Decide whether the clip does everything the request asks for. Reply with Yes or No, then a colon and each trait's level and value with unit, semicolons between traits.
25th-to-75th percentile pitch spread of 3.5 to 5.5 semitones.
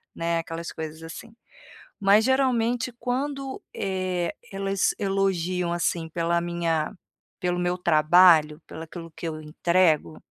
No: average, 3.1 semitones